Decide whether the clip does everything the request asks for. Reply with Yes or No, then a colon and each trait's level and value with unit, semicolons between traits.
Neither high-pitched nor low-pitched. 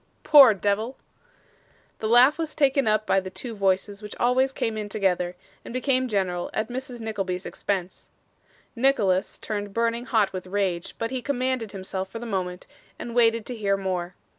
No: high, 215 Hz